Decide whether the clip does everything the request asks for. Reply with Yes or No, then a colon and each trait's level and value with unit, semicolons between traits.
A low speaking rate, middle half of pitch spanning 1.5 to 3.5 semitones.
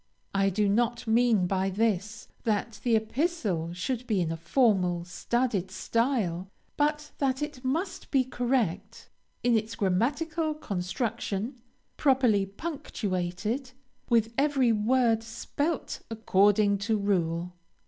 No: slow, 115 wpm; average, 4.9 semitones